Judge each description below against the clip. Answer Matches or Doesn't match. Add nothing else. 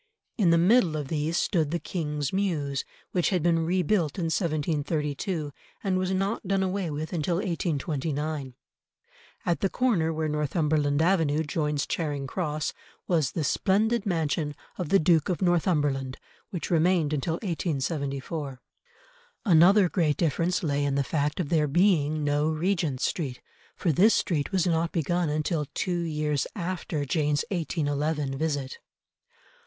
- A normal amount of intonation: Matches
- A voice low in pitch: Doesn't match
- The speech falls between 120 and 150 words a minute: Matches